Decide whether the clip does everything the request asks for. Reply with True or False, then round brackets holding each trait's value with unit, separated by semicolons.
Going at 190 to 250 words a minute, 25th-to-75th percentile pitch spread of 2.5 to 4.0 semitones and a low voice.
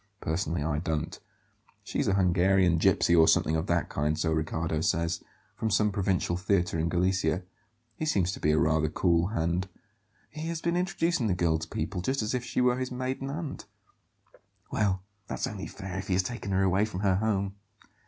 False (195 wpm; 4.4 semitones; 95 Hz)